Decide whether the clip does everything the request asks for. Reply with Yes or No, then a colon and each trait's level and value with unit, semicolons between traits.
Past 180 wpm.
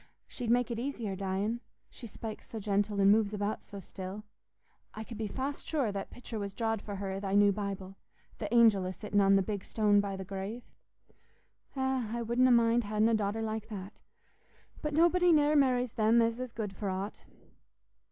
Yes: average, 190 wpm